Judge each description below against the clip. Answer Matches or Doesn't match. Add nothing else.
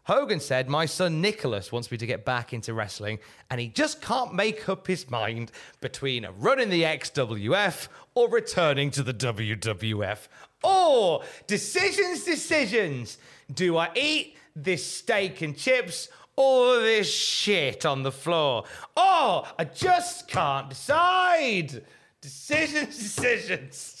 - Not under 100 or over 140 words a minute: Matches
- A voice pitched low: Doesn't match